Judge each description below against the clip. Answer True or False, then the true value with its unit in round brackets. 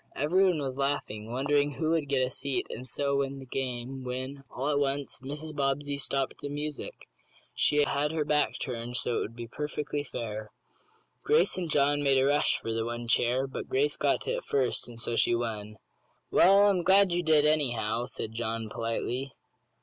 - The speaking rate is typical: True (190 wpm)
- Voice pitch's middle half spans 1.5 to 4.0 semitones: True (3.5 semitones)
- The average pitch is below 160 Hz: True (135 Hz)